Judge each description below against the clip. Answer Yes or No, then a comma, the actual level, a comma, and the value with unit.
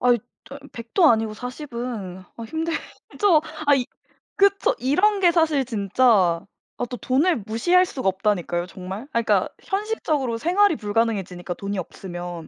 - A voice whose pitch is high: Yes, high, 240 Hz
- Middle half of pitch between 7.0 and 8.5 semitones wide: Yes, wide, 8.2 semitones